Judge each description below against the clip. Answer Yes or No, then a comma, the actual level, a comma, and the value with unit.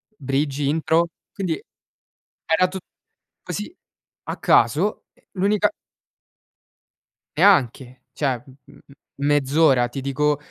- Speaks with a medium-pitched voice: Yes, medium, 145 Hz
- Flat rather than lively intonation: No, average, 3.9 semitones